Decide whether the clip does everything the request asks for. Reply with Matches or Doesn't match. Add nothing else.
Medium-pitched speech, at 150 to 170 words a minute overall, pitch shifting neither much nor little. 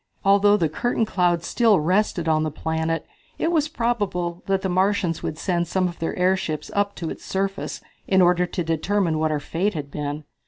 Doesn't match